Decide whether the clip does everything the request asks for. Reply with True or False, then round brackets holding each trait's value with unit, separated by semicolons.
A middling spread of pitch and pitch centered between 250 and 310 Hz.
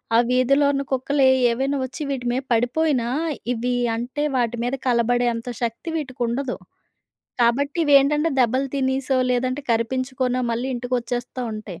False (2.3 semitones; 255 Hz)